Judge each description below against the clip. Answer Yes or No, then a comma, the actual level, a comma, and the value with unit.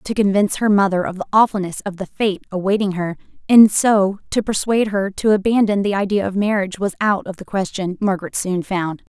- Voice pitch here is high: Yes, high, 195 Hz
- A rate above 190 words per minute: Yes, average, 200 wpm